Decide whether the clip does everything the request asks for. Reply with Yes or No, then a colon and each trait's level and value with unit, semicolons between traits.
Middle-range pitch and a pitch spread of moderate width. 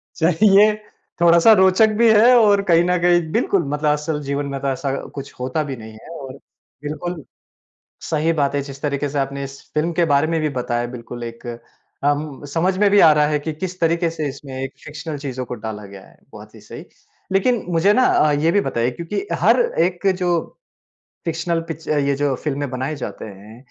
Yes: medium, 150 Hz; average, 3.9 semitones